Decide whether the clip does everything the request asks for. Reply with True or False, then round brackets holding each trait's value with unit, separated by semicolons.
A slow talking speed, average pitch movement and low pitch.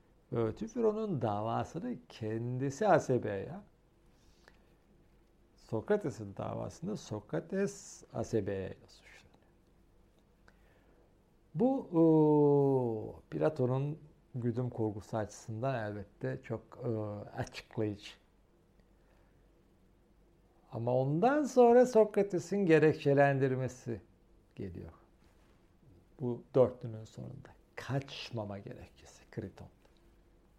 False (60 wpm; 5.8 semitones; 125 Hz)